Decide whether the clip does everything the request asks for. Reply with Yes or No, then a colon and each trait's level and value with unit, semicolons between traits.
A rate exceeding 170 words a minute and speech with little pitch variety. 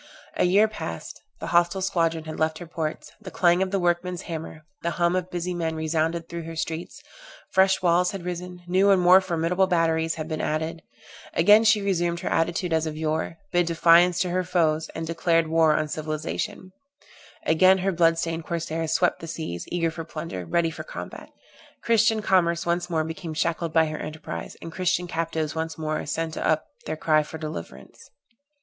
Yes: average, 185 wpm; narrow, 2.0 semitones